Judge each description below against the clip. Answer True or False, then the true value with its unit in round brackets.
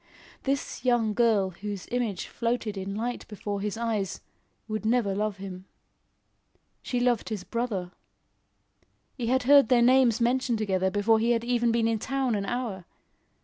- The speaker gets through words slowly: False (150 wpm)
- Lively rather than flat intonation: False (3.2 semitones)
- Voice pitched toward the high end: True (225 Hz)